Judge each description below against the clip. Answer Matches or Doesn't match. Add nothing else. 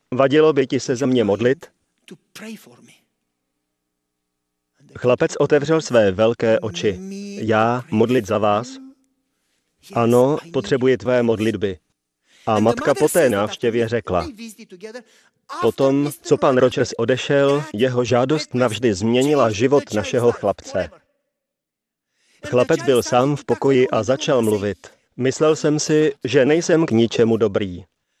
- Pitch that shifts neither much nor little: Matches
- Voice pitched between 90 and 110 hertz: Doesn't match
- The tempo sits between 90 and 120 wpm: Matches